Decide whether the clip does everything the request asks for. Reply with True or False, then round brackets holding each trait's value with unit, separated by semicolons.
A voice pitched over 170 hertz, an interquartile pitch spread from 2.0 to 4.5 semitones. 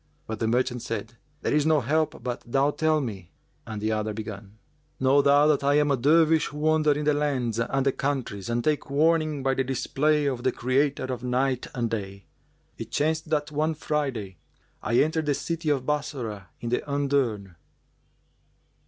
False (135 Hz; 4.2 semitones)